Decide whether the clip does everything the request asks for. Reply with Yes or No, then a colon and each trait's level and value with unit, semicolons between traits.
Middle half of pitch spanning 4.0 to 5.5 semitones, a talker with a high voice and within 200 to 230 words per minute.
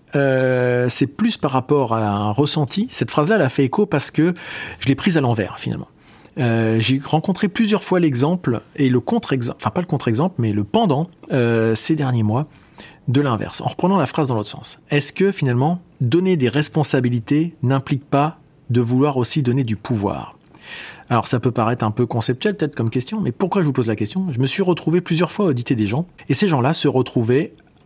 No: average, 4.7 semitones; medium, 140 Hz; average, 205 wpm